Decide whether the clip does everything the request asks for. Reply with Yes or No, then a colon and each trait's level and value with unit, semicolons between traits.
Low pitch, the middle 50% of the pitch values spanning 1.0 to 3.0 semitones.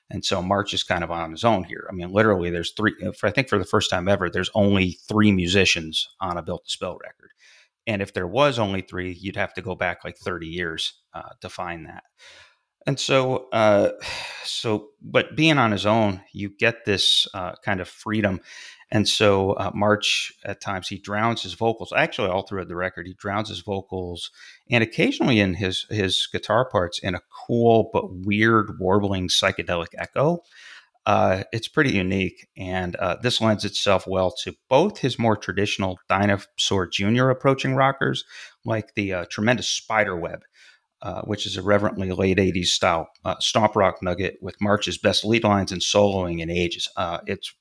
Yes: low, 100 Hz; average, 2.7 semitones